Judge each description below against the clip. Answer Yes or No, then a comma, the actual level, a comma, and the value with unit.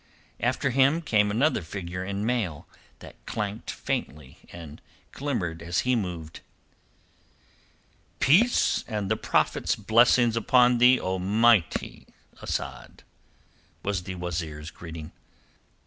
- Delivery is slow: Yes, slow, 110 wpm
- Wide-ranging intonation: Yes, wide, 5.9 semitones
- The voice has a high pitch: No, low, 100 Hz